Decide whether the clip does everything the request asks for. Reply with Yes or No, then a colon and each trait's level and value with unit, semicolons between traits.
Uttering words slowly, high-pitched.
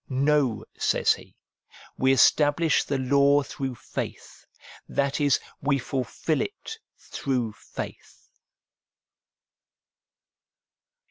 No: slow, 90 wpm; medium, 140 Hz